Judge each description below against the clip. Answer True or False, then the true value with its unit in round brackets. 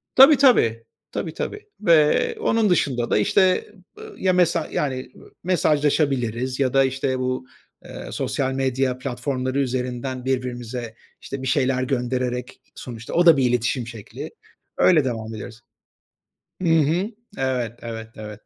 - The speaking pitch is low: True (130 Hz)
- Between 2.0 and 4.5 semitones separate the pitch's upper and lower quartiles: True (3.5 semitones)